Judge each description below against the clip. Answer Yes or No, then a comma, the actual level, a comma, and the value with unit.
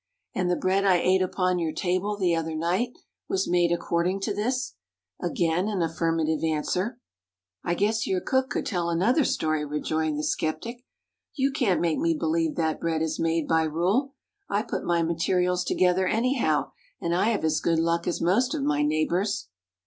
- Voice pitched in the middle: Yes, medium, 175 Hz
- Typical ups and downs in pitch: Yes, average, 3.4 semitones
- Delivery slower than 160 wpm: No, average, 180 wpm